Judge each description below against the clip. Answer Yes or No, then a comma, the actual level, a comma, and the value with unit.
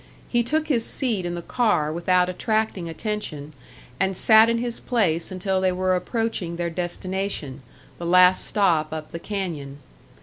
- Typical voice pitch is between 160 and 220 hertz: Yes, medium, 185 Hz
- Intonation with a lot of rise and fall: No, average, 4.3 semitones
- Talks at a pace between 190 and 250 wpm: No, average, 160 wpm